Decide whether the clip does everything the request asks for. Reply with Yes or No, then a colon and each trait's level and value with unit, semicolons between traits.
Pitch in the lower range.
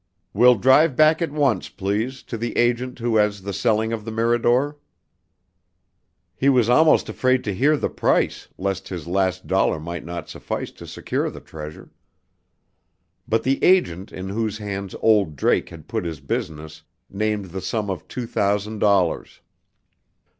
Yes: low, 105 Hz